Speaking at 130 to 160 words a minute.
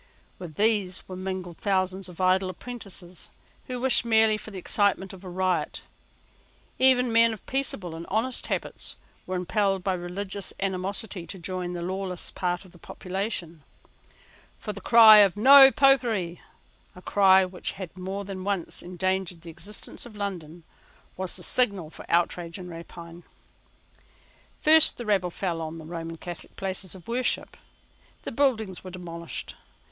Yes: average, 155 wpm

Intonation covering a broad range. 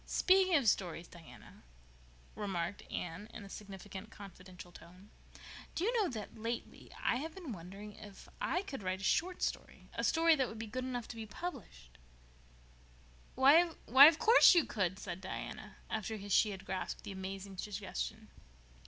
Yes: wide, 5.8 semitones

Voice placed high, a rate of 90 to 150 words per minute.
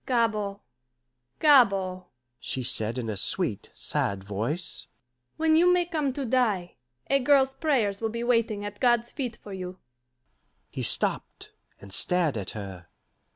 Yes: high, 205 Hz; average, 145 wpm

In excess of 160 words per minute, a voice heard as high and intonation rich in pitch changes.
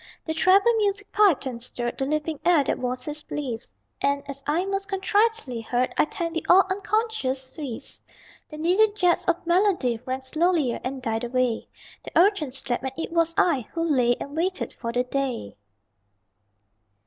Yes: average, 170 wpm; very high, 305 Hz; wide, 6.3 semitones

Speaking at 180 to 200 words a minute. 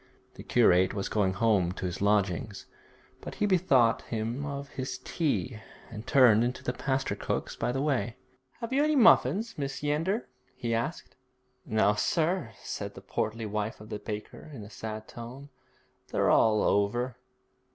No: average, 160 wpm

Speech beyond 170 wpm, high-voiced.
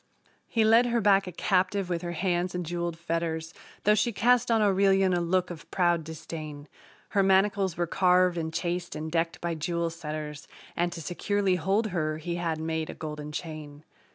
No: average, 185 wpm; medium, 175 Hz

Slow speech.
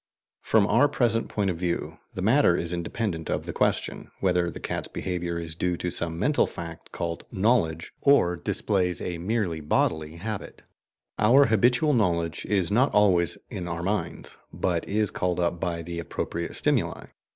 No: average, 165 wpm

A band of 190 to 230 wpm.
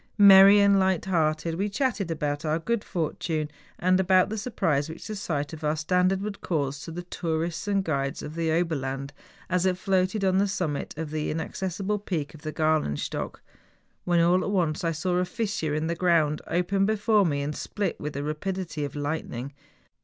Yes: average, 195 wpm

